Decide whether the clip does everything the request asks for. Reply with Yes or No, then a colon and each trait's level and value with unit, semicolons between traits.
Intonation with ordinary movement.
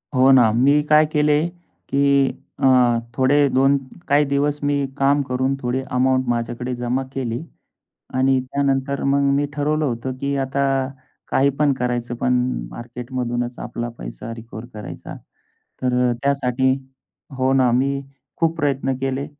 No: narrow, 2.2 semitones